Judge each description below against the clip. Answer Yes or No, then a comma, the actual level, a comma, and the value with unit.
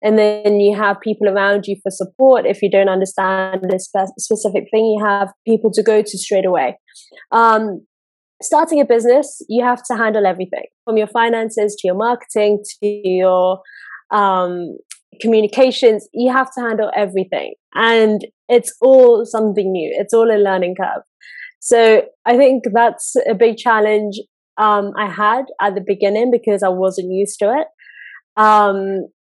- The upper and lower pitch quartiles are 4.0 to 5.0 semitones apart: No, average, 2.8 semitones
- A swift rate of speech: No, average, 160 wpm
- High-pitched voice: Yes, high, 215 Hz